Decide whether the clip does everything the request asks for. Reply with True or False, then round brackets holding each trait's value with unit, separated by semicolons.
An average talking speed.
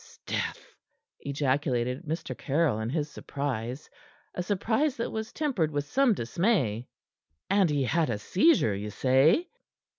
False (130 wpm)